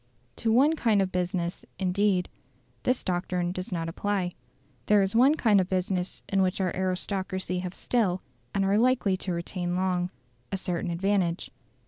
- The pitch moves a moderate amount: No, narrow, 2.1 semitones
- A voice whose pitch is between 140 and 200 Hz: Yes, medium, 185 Hz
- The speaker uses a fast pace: No, average, 160 wpm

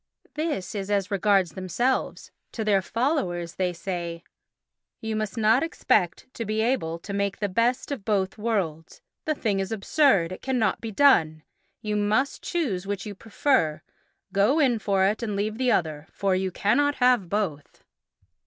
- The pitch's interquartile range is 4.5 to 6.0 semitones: No, average, 4.0 semitones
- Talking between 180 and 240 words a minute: No, average, 165 wpm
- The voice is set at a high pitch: Yes, high, 205 Hz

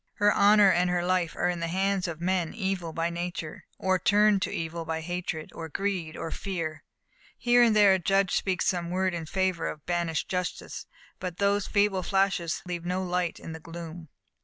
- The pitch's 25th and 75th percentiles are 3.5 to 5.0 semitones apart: No, narrow, 2.5 semitones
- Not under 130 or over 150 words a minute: No, average, 195 wpm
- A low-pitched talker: No, medium, 180 Hz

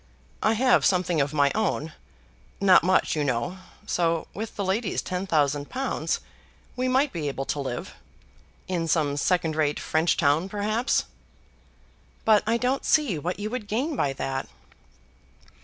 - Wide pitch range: Yes, wide, 6.7 semitones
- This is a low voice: No, medium, 180 Hz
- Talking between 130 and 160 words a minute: Yes, average, 155 wpm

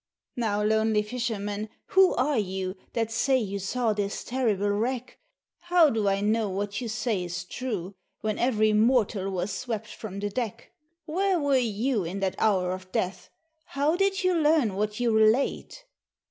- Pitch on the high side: Yes, high, 220 Hz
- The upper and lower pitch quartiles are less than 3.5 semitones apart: No, average, 4.0 semitones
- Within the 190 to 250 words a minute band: No, average, 165 wpm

